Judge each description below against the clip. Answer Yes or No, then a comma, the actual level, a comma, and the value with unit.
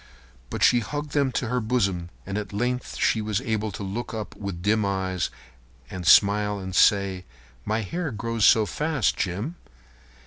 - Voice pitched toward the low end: Yes, low, 105 Hz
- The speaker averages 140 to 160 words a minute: No, average, 175 wpm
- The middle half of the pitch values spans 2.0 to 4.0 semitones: Yes, average, 3.6 semitones